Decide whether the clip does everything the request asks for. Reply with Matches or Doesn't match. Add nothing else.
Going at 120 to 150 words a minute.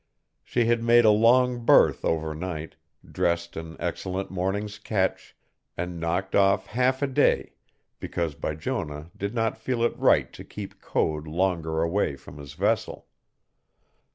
Matches